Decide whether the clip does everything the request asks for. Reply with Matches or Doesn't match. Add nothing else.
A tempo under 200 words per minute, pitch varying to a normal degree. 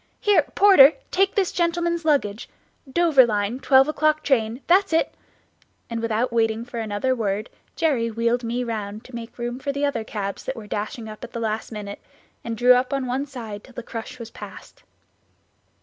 Matches